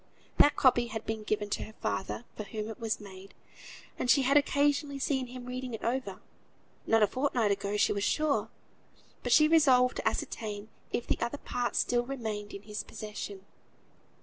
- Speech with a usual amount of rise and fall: Yes, average, 3.8 semitones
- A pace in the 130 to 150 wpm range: No, average, 180 wpm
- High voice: Yes, high, 230 Hz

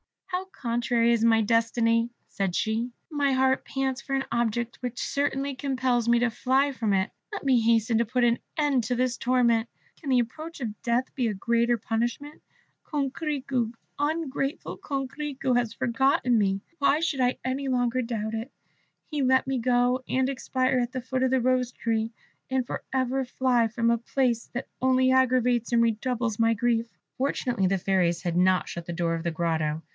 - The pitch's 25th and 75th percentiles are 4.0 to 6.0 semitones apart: No, narrow, 2.5 semitones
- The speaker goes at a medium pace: Yes, average, 180 wpm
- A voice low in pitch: No, high, 245 Hz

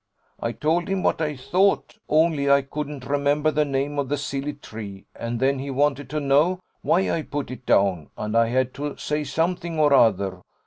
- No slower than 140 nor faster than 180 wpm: No, average, 195 wpm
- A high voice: No, medium, 140 Hz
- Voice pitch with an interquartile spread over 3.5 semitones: No, average, 2.8 semitones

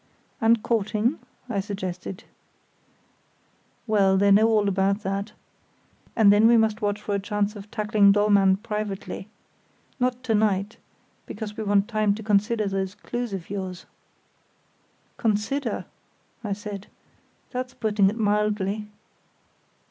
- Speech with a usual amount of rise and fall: No, narrow, 1.7 semitones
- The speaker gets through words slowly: Yes, slow, 125 wpm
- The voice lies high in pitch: Yes, high, 210 Hz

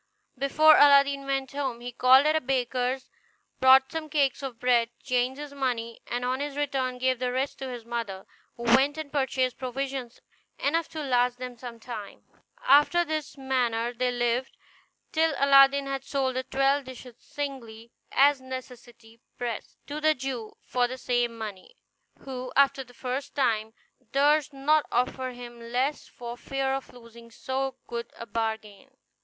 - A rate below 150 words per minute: No, average, 160 wpm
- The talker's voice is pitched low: No, very high, 260 Hz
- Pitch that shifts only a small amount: Yes, narrow, 2.3 semitones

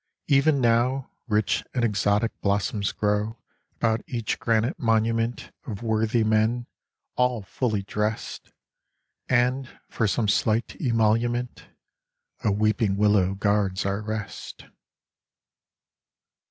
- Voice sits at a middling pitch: No, low, 110 Hz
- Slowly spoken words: Yes, slow, 105 wpm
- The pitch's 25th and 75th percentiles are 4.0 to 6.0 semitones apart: No, narrow, 2.4 semitones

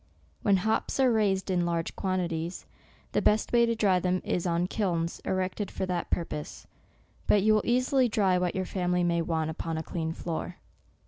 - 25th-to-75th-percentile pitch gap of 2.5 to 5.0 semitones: Yes, average, 3.5 semitones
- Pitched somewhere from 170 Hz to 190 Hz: Yes, medium, 185 Hz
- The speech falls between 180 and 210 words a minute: Yes, average, 185 wpm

